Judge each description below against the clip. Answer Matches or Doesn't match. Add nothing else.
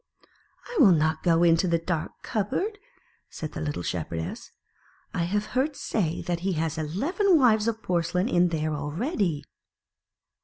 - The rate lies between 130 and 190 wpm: Matches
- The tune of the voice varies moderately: Doesn't match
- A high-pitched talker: Doesn't match